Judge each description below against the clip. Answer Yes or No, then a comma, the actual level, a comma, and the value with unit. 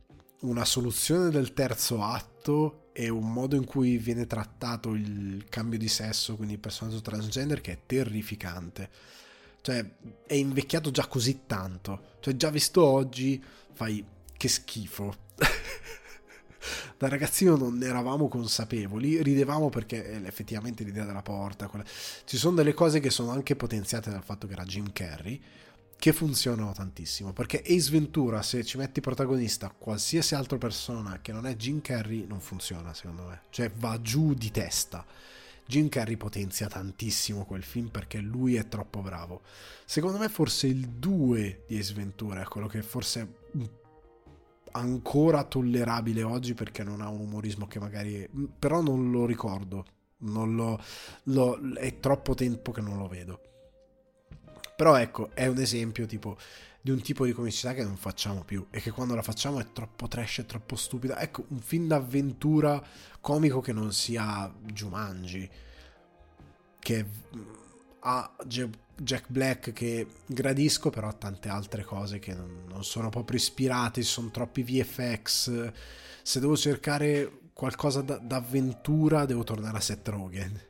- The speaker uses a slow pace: No, average, 150 wpm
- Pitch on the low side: Yes, low, 115 Hz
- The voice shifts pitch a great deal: No, average, 4.3 semitones